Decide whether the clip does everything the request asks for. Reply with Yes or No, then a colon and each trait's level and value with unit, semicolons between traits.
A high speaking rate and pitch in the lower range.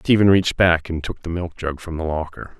Yes: fast, 230 wpm; very low, 85 Hz